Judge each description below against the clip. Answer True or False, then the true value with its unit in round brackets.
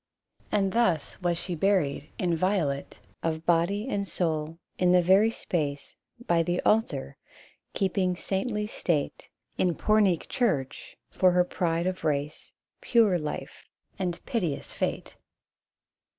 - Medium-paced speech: False (120 wpm)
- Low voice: False (180 Hz)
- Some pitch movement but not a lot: True (3.1 semitones)